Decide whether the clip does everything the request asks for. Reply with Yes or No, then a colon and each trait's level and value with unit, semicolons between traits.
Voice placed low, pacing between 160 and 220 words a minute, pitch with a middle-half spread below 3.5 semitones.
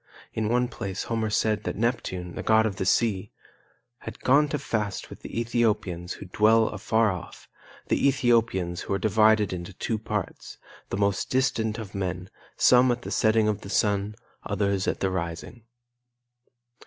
Yes: low, 105 Hz; average, 165 wpm; average, 3.0 semitones